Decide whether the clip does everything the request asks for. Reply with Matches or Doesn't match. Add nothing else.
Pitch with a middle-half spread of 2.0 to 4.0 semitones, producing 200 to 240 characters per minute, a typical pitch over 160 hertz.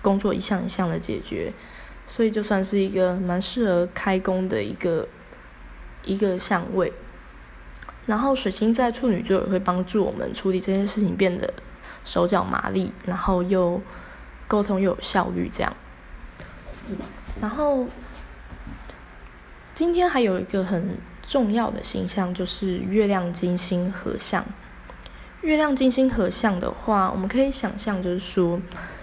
Matches